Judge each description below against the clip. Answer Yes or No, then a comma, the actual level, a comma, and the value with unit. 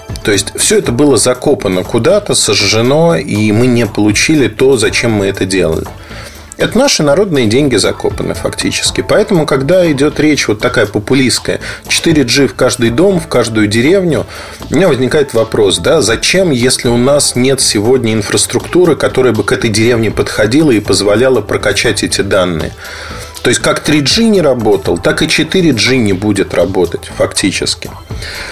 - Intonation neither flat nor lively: No, wide, 6.2 semitones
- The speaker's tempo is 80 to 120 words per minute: No, average, 155 wpm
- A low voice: Yes, low, 130 Hz